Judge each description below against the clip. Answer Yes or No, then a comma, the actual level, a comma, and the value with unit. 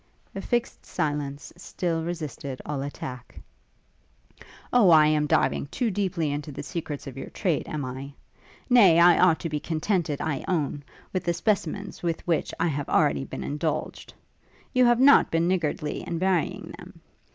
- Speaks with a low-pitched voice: No, medium, 160 Hz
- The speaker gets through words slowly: No, average, 165 wpm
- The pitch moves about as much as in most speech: Yes, average, 3.9 semitones